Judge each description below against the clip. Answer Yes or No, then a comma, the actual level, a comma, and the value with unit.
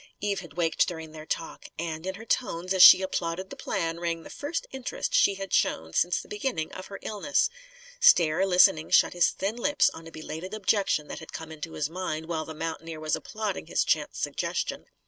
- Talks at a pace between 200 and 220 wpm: Yes, fast, 205 wpm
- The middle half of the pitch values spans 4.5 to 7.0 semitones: No, average, 3.8 semitones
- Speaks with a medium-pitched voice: Yes, medium, 175 Hz